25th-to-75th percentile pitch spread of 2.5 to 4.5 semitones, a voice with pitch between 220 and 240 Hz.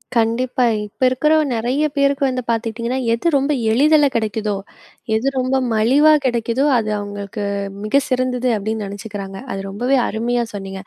Yes: average, 3.3 semitones; high, 235 Hz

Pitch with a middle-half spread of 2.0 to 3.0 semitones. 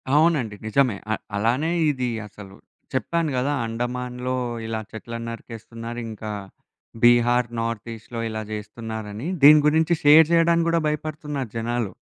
No: average, 4.7 semitones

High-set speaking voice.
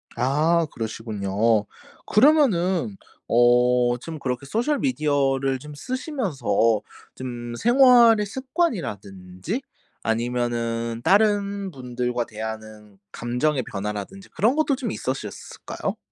No: low, 130 Hz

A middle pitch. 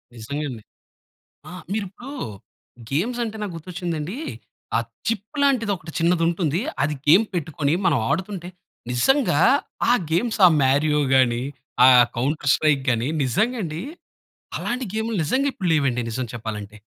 Yes: medium, 165 Hz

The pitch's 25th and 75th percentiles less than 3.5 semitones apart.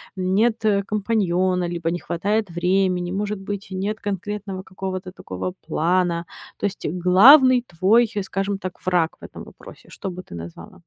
Yes: narrow, 2.4 semitones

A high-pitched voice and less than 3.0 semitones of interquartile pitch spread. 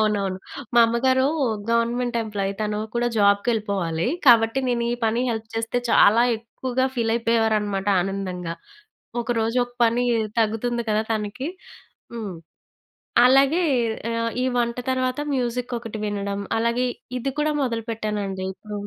Yes: high, 225 Hz; narrow, 2.6 semitones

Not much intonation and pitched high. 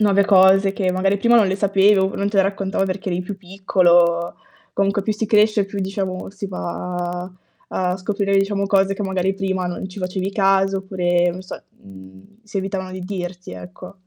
Yes: narrow, 1.4 semitones; high, 195 Hz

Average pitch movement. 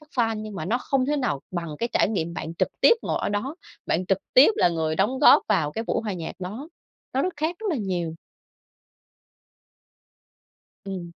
No: wide, 7.2 semitones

